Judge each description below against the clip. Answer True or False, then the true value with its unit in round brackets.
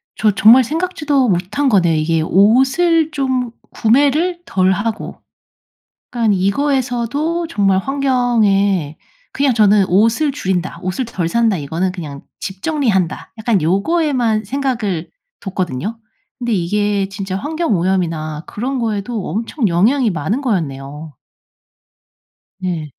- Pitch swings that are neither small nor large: False (6.0 semitones)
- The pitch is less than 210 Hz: False (215 Hz)